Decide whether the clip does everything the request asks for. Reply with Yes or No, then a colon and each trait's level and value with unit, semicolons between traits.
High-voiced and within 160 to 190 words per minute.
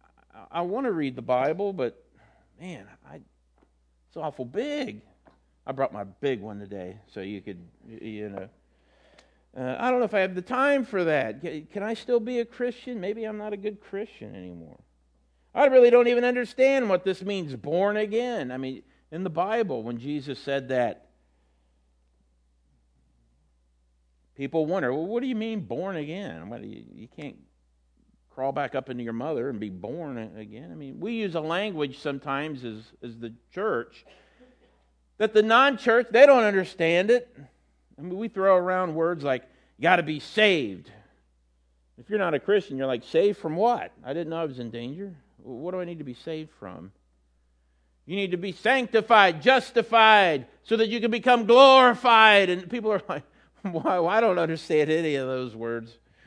No: medium, 160 Hz; average, 175 wpm